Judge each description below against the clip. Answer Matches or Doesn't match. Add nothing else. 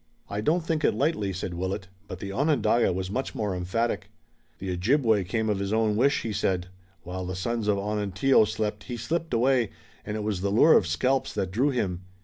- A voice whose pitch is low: Matches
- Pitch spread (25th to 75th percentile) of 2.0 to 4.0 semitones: Doesn't match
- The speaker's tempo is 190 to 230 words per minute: Matches